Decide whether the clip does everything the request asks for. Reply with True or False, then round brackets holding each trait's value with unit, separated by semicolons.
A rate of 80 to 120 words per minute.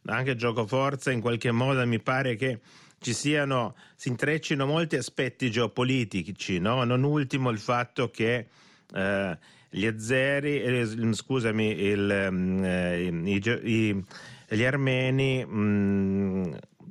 True (115 wpm)